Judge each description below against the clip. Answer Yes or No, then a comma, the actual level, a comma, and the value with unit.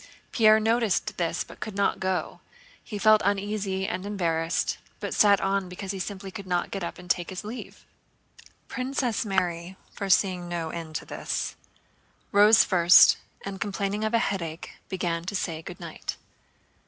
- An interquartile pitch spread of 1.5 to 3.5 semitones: Yes, average, 2.8 semitones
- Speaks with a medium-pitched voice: No, high, 195 Hz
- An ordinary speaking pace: Yes, average, 160 wpm